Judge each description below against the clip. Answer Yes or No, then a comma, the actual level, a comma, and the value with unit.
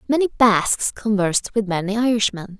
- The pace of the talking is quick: No, average, 140 wpm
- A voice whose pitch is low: No, high, 215 Hz